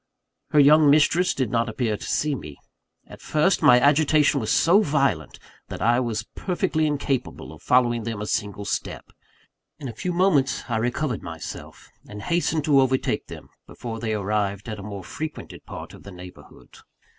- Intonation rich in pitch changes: Yes, wide, 6.0 semitones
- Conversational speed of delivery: Yes, average, 175 wpm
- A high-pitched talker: No, low, 125 Hz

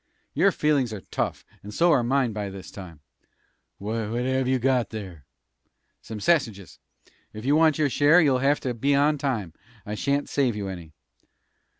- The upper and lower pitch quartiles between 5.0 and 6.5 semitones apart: Yes, average, 5.3 semitones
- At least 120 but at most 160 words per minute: No, average, 175 wpm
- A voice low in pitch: Yes, low, 125 Hz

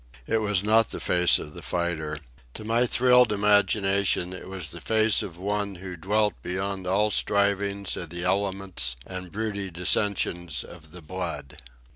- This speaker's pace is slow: No, average, 160 wpm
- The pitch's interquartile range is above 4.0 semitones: No, average, 2.8 semitones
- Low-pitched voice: Yes, very low, 95 Hz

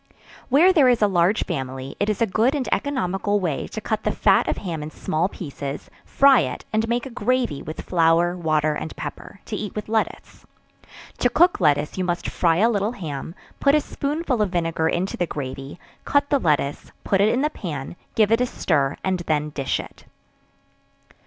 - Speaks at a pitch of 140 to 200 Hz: Yes, medium, 185 Hz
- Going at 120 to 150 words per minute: No, average, 195 wpm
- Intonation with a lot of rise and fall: Yes, wide, 6.7 semitones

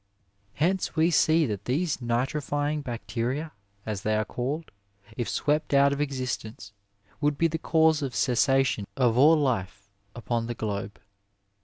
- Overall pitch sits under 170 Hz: Yes, low, 135 Hz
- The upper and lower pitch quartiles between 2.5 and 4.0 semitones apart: No, average, 4.6 semitones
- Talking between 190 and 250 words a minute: No, average, 145 wpm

